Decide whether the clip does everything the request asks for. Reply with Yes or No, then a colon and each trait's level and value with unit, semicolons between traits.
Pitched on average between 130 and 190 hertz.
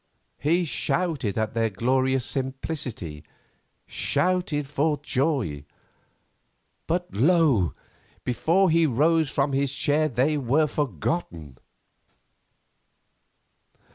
Yes: medium, 140 Hz